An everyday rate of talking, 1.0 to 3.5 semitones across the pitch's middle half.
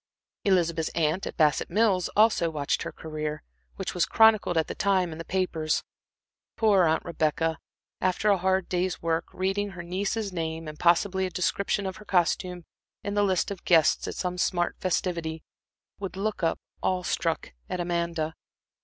Yes: average, 170 wpm; average, 2.8 semitones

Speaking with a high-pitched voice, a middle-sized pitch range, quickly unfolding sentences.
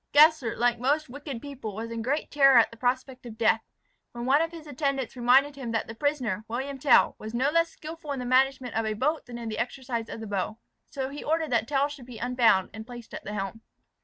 Yes: very high, 255 Hz; average, 3.7 semitones; fast, 240 wpm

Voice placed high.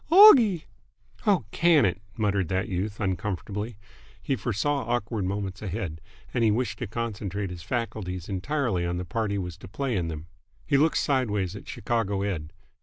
No: low, 105 Hz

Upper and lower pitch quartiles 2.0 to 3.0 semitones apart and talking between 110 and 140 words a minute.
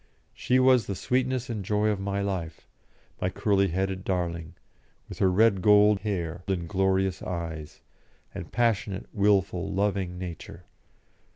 Yes: narrow, 2.6 semitones; slow, 135 wpm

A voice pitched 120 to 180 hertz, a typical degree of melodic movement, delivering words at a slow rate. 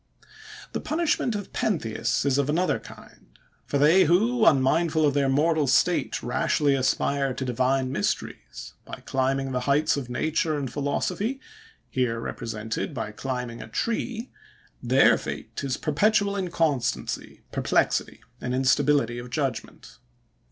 Yes: medium, 140 Hz; average, 4.6 semitones; slow, 130 wpm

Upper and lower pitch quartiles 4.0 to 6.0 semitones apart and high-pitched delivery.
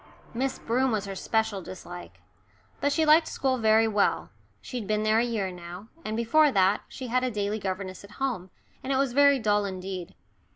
Yes: average, 4.6 semitones; high, 220 Hz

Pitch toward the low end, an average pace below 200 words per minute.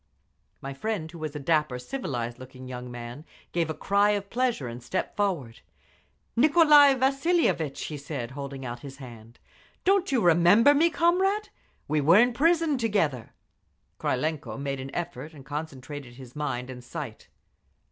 No: medium, 155 Hz; average, 155 wpm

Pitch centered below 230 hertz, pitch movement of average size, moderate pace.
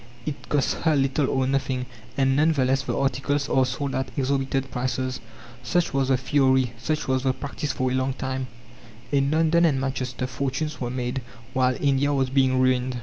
No: low, 135 Hz; narrow, 1.3 semitones; average, 190 wpm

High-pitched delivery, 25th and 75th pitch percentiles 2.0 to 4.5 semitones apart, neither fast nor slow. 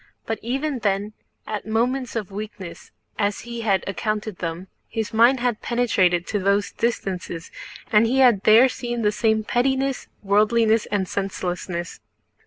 Yes: high, 215 Hz; average, 3.3 semitones; average, 145 wpm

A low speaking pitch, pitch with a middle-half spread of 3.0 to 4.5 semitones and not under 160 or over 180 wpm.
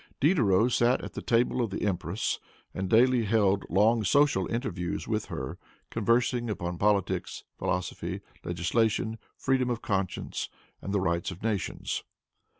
No: low, 105 Hz; average, 4.0 semitones; average, 140 wpm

